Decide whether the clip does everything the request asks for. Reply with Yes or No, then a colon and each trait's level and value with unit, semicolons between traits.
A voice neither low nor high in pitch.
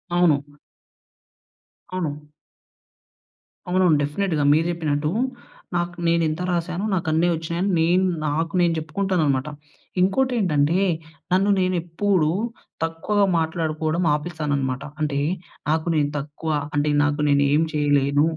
Yes: medium, 160 Hz